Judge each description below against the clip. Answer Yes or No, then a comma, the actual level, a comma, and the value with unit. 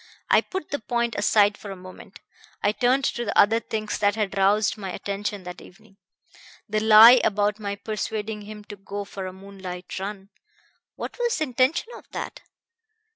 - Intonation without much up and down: Yes, narrow, 1.9 semitones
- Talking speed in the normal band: Yes, average, 180 wpm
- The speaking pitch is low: No, high, 210 Hz